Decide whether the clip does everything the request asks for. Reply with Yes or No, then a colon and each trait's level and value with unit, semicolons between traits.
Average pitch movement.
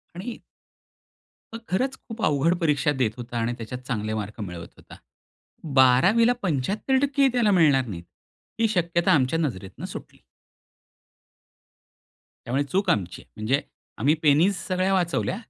No: wide, 8.0 semitones